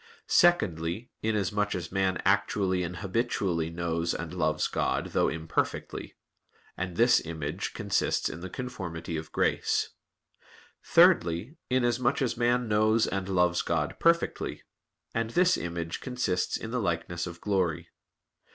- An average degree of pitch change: No, wide, 5.7 semitones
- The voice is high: No, very low, 95 Hz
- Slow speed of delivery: Yes, slow, 130 wpm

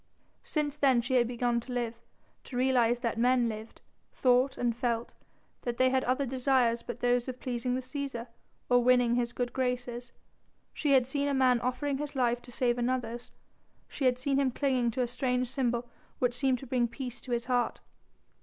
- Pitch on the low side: No, high, 245 Hz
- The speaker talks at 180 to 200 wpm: Yes, average, 190 wpm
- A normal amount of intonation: No, narrow, 1.4 semitones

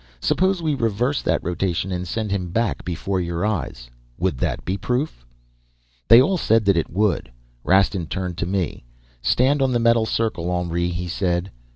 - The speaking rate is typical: Yes, average, 175 wpm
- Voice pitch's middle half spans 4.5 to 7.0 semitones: Yes, average, 4.9 semitones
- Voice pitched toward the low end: Yes, very low, 95 Hz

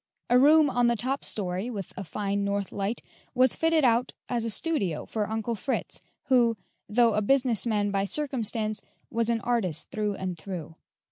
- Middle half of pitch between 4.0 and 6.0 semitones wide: No, average, 3.6 semitones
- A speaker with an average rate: Yes, average, 180 wpm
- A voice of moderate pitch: No, high, 225 Hz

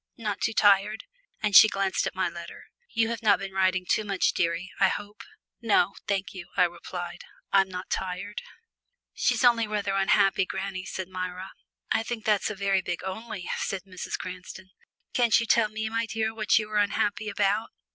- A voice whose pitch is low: No, high, 200 Hz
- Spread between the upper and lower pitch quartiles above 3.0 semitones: No, narrow, 2.5 semitones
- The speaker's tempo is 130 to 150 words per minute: No, average, 185 wpm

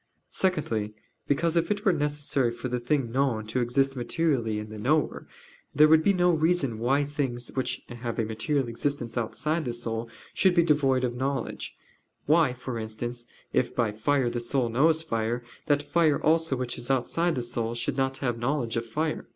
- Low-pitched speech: Yes, low, 130 Hz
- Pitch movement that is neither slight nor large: Yes, average, 4.3 semitones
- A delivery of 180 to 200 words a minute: Yes, average, 185 wpm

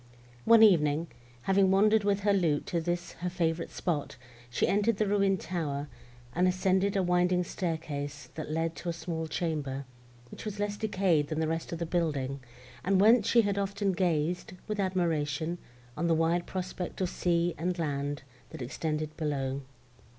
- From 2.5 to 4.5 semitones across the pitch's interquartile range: Yes, average, 3.7 semitones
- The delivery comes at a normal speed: Yes, average, 170 wpm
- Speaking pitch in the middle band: Yes, medium, 175 Hz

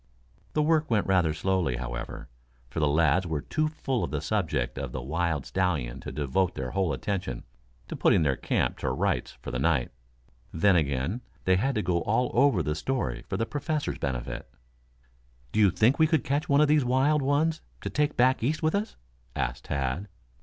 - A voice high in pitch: No, very low, 95 Hz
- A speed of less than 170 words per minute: No, average, 195 wpm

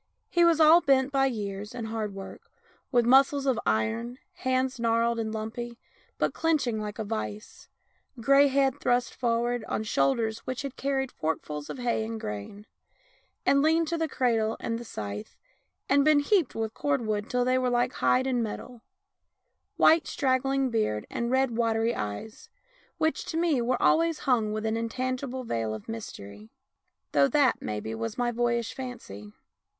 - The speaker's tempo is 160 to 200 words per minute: Yes, average, 170 wpm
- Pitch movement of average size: Yes, average, 3.6 semitones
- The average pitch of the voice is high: Yes, high, 240 Hz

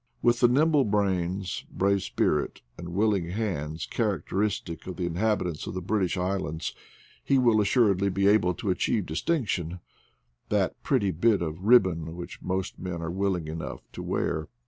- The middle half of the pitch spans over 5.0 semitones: No, average, 3.7 semitones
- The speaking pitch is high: No, very low, 95 Hz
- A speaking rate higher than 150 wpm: Yes, average, 165 wpm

